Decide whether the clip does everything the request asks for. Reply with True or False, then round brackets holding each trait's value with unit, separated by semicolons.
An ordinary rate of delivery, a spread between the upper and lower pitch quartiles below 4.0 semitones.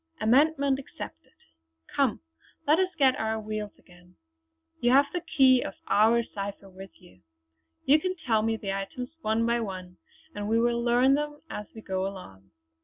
False (175 wpm; 5.3 semitones)